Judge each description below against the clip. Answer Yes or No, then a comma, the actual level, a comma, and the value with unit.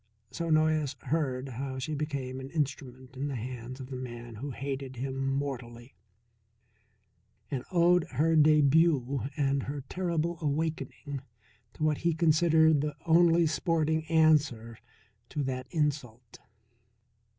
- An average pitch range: Yes, average, 3.4 semitones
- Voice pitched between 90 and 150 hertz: Yes, medium, 140 Hz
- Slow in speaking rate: Yes, slow, 130 wpm